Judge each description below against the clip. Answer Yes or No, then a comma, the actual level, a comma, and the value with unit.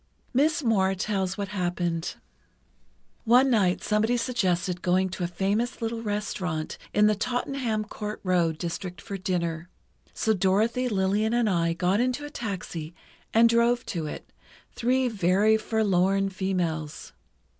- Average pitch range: Yes, average, 4.2 semitones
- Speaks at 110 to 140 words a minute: Yes, slow, 135 wpm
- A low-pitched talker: No, high, 200 Hz